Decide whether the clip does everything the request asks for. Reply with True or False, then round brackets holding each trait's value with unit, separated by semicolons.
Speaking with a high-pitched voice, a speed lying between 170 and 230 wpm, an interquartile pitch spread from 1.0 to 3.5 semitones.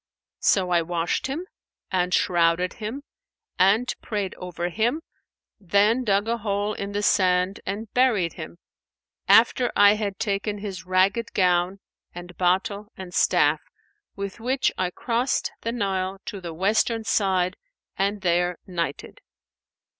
False (195 Hz; 135 wpm; 3.1 semitones)